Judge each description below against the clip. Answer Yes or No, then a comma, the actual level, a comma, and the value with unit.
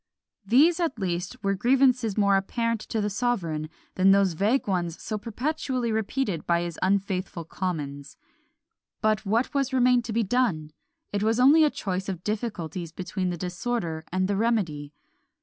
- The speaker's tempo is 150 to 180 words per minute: Yes, average, 155 wpm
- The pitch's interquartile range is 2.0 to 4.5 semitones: No, average, 5.1 semitones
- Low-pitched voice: No, high, 200 Hz